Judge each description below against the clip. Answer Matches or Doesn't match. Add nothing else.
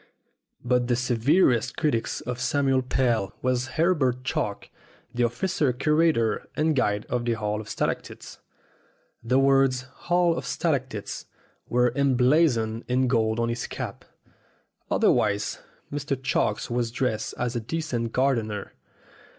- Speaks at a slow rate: Matches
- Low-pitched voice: Matches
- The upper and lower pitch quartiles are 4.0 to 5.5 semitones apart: Doesn't match